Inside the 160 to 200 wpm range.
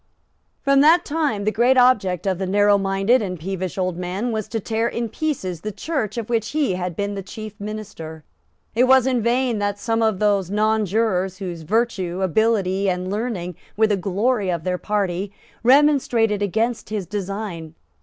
Yes: average, 175 wpm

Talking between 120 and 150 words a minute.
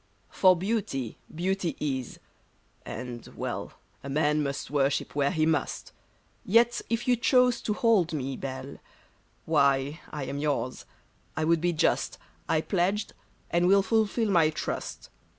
Yes: average, 145 wpm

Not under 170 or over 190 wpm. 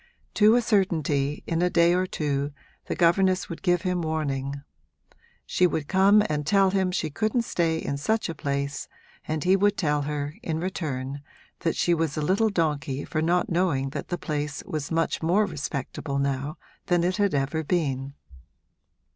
Yes: average, 175 wpm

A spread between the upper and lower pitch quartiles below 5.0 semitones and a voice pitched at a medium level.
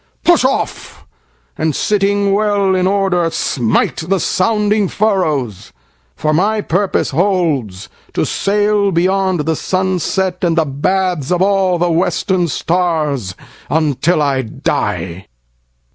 Yes: average, 4.2 semitones; medium, 180 Hz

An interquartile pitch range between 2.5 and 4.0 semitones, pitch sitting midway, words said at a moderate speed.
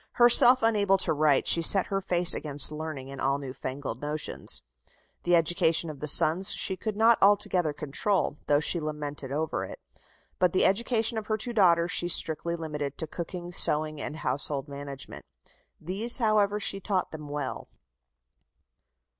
No: average, 5.0 semitones; medium, 165 Hz; average, 165 wpm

